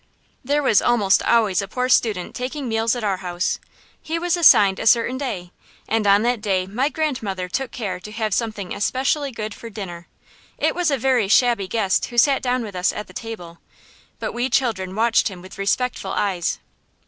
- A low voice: No, high, 225 Hz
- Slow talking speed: No, average, 190 wpm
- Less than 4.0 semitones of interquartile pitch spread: No, average, 4.5 semitones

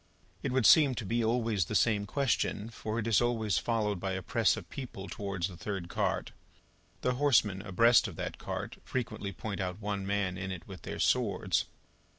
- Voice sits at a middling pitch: No, low, 105 Hz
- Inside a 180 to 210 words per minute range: Yes, average, 190 wpm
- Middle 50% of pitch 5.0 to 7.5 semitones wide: No, average, 3.4 semitones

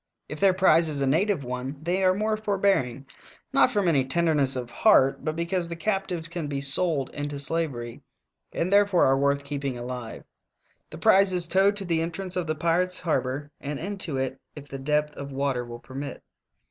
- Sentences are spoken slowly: No, average, 195 wpm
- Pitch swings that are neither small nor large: Yes, average, 5.0 semitones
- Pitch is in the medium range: Yes, medium, 155 Hz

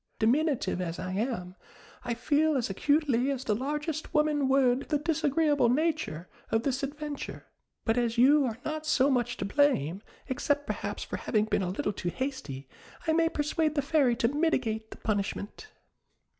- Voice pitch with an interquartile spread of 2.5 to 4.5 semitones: No, average, 5.1 semitones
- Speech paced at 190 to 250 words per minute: No, average, 170 wpm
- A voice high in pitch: Yes, very high, 265 Hz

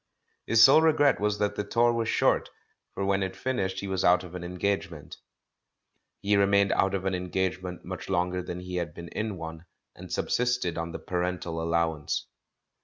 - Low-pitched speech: Yes, very low, 95 Hz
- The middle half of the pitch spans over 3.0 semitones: No, narrow, 2.6 semitones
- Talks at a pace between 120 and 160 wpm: No, average, 180 wpm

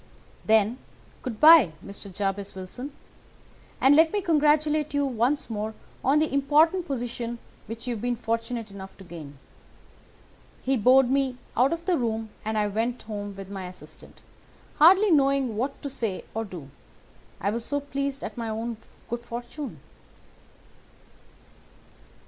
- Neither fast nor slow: Yes, average, 150 wpm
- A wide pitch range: No, average, 4.7 semitones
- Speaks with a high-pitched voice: Yes, high, 240 Hz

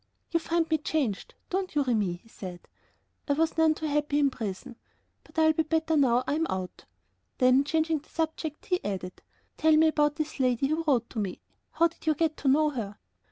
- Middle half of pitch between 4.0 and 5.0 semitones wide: Yes, average, 4.5 semitones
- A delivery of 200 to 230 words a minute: Yes, fast, 205 wpm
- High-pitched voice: Yes, very high, 295 Hz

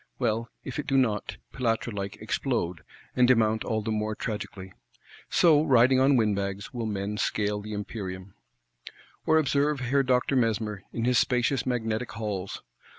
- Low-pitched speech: Yes, low, 115 Hz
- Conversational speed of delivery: Yes, average, 150 wpm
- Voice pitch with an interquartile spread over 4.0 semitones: No, average, 3.7 semitones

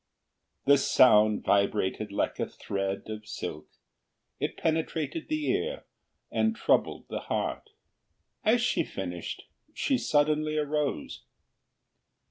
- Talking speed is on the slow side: Yes, slow, 105 wpm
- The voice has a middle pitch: Yes, medium, 150 Hz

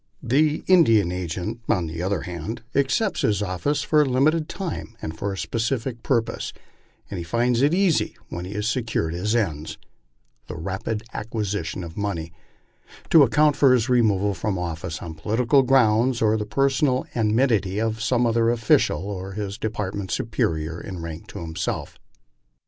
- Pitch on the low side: Yes, low, 110 Hz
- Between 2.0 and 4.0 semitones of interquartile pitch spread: No, average, 5.3 semitones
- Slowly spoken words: No, average, 160 wpm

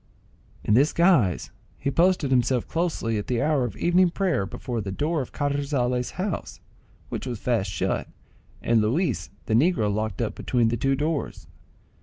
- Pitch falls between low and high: No, low, 130 Hz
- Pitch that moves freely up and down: Yes, wide, 5.9 semitones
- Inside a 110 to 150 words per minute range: No, average, 165 wpm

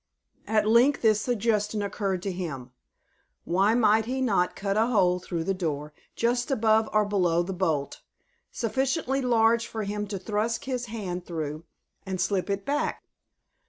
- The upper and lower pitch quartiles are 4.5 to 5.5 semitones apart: No, average, 4.1 semitones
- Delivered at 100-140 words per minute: No, average, 160 wpm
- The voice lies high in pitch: Yes, high, 210 Hz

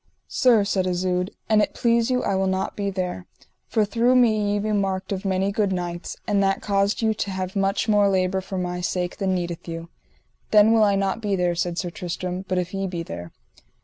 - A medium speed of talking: No, fast, 220 wpm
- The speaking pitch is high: Yes, high, 195 Hz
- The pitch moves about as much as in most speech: No, narrow, 2.3 semitones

